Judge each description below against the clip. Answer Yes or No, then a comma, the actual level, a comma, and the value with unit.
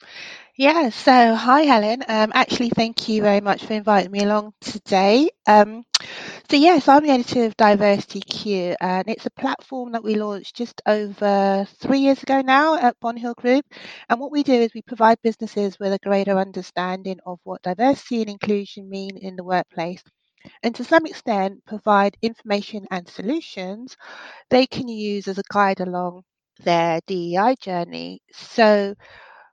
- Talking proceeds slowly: No, average, 165 wpm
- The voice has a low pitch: No, high, 215 Hz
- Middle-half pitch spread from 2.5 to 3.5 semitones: No, average, 4.0 semitones